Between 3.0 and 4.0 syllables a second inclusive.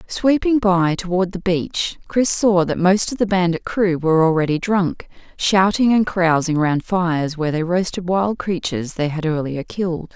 No: 4.9 syllables/s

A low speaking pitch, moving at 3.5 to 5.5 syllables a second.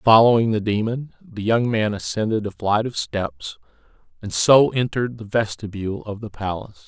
Yes: low, 110 Hz; 5.1 syllables/s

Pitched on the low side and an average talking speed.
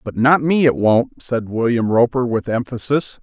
Yes: low, 125 Hz; average, 185 wpm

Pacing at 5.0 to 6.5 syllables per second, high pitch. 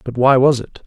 No: 5.3 syllables/s; low, 130 Hz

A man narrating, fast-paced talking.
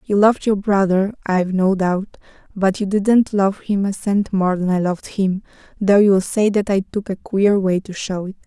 No: female; fast, 220 wpm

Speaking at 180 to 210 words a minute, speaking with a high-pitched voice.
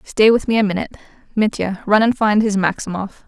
Yes: average, 200 wpm; high, 210 Hz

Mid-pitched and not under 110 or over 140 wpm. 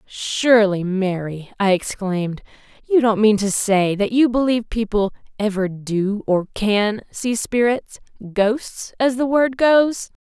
No: high, 215 Hz; slow, 135 wpm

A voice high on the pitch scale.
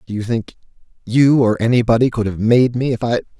No: low, 115 Hz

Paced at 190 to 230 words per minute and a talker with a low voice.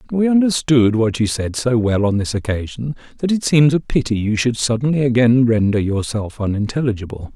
No: average, 180 wpm; low, 120 Hz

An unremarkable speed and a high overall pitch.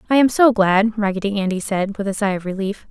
No: fast, 250 wpm; high, 205 Hz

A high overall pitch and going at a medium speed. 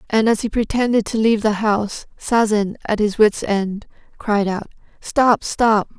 Yes: high, 215 Hz; average, 170 wpm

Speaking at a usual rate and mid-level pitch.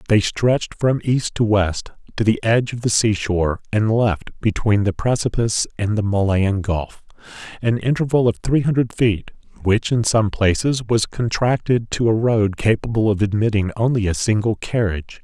No: average, 175 wpm; low, 110 Hz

